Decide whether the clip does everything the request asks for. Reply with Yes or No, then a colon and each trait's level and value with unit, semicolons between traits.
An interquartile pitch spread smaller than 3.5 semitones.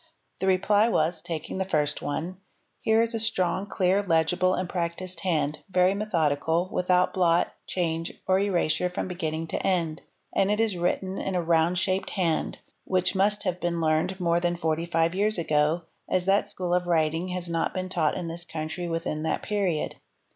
Yes: narrow, 2.4 semitones